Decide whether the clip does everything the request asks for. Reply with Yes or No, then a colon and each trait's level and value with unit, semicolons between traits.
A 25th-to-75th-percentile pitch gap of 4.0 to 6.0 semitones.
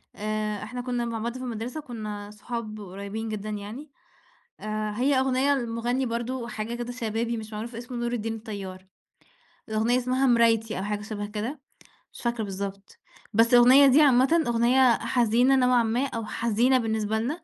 No: average, 2.7 semitones